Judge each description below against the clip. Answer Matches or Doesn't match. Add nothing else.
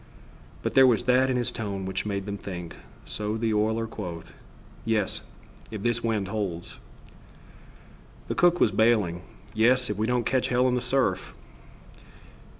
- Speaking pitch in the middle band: Doesn't match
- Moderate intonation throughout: Matches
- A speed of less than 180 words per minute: Matches